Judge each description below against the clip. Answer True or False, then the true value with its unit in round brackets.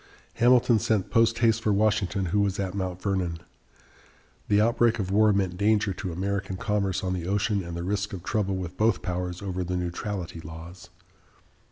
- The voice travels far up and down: False (2.8 semitones)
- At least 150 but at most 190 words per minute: True (180 wpm)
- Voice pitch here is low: True (100 Hz)